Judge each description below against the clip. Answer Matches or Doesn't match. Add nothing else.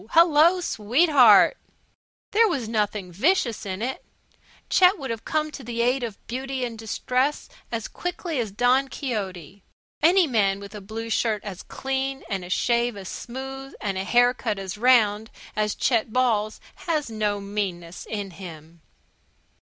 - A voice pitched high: Matches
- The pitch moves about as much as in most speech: Matches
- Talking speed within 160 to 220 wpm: Doesn't match